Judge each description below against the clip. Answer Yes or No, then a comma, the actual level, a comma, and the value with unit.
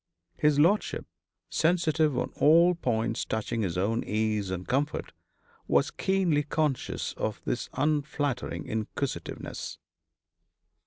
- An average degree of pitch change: No, wide, 5.9 semitones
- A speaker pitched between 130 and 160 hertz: Yes, medium, 140 Hz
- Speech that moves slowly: Yes, slow, 105 wpm